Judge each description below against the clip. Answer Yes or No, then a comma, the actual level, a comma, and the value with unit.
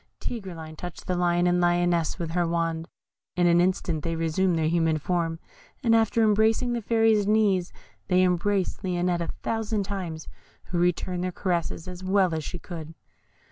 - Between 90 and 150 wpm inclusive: No, average, 170 wpm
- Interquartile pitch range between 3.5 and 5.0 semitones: No, average, 2.7 semitones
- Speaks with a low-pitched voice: No, medium, 180 Hz